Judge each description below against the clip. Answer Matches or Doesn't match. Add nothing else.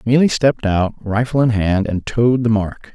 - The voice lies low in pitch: Matches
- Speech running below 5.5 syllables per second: Matches